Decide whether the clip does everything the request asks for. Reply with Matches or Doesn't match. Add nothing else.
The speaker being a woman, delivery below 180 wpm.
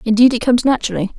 Doesn't match